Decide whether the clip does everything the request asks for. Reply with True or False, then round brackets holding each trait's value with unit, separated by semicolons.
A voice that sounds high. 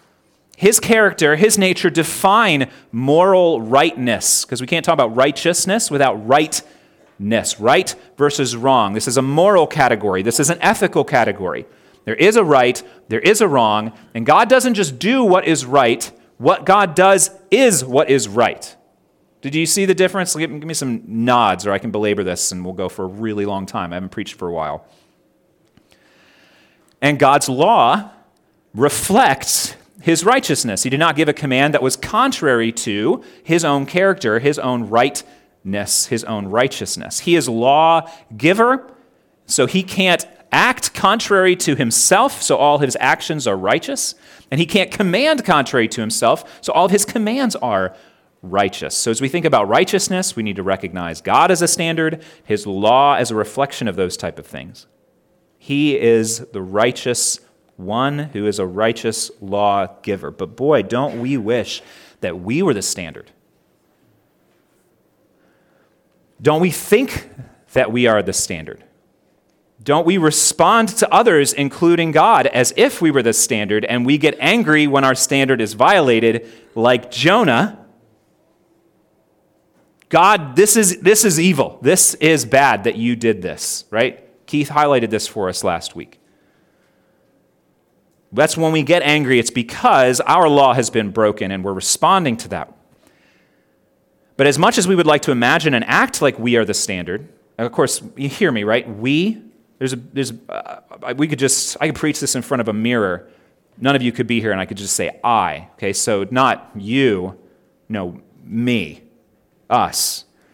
False (140 Hz)